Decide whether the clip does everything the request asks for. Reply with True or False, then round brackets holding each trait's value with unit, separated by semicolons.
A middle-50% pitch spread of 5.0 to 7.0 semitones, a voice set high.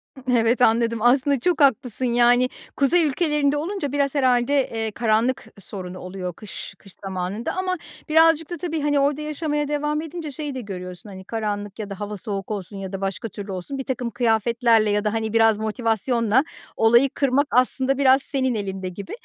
True (5.3 semitones; 240 Hz)